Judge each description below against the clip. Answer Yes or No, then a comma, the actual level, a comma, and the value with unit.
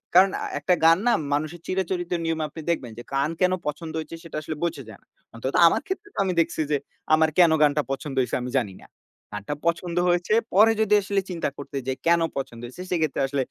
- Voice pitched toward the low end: No, medium, 160 Hz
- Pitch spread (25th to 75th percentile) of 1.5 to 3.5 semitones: No, average, 4.1 semitones